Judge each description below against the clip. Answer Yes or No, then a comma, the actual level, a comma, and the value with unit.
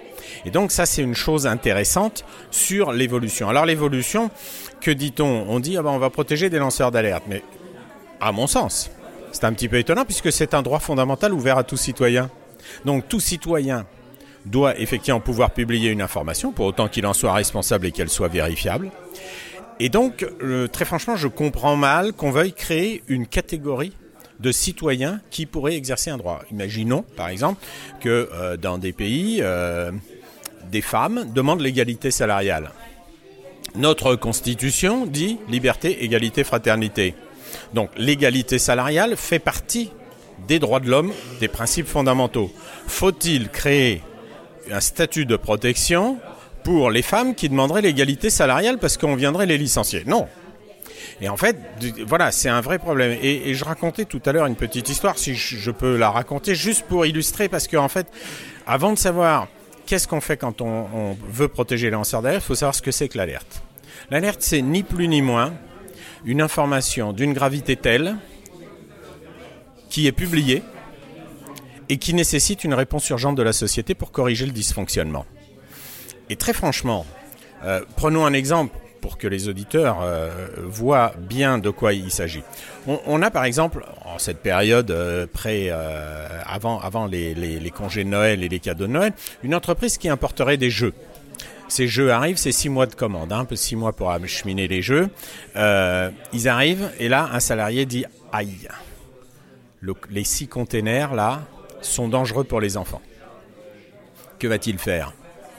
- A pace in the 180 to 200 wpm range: No, average, 170 wpm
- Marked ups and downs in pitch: Yes, wide, 6.0 semitones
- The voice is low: Yes, low, 130 Hz